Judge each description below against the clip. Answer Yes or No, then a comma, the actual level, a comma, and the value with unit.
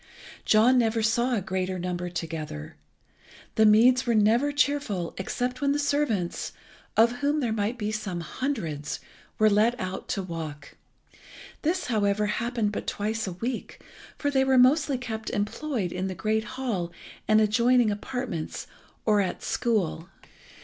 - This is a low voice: No, high, 220 Hz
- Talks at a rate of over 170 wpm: No, average, 150 wpm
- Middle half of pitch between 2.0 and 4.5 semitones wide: No, average, 4.9 semitones